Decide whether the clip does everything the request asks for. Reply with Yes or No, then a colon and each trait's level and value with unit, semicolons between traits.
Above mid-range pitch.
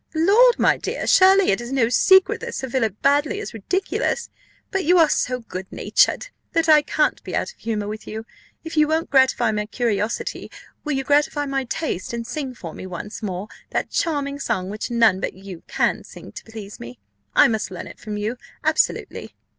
Yes: high, 245 Hz